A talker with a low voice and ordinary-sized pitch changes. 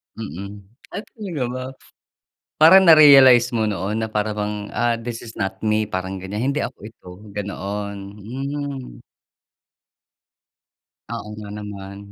Yes: low, 110 Hz; average, 4.2 semitones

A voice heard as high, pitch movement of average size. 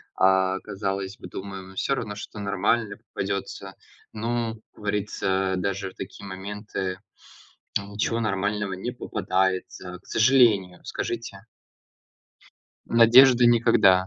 No: low, 100 Hz; average, 3.0 semitones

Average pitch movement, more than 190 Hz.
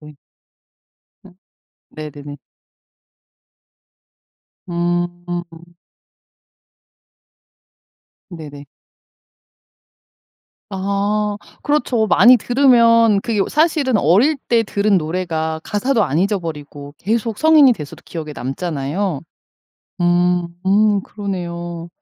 No: average, 4.8 semitones; medium, 185 Hz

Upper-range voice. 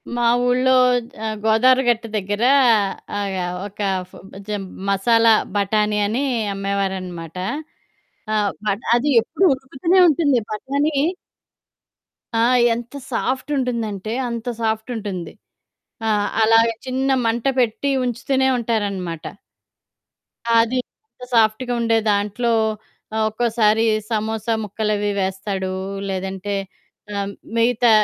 Yes: high, 220 Hz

